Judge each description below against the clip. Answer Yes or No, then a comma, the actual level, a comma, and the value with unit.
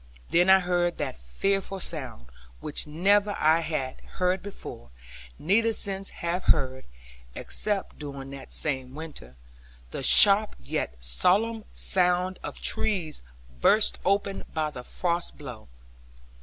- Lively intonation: Yes, wide, 6.0 semitones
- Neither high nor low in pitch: Yes, medium, 175 Hz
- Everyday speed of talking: No, slow, 125 wpm